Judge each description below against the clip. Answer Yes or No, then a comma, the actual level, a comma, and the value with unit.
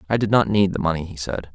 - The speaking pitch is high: No, very low, 90 Hz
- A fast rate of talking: Yes, fast, 310 wpm